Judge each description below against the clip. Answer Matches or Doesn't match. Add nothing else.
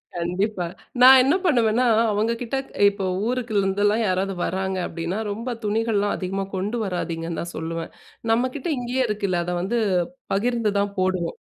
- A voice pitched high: Matches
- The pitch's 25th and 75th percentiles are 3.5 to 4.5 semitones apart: Matches